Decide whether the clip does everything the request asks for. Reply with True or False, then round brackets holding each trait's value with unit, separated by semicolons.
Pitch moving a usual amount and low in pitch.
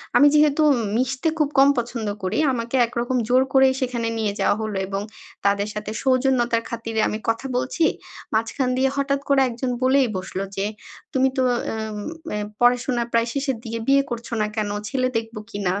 False (3.1 semitones; 240 Hz)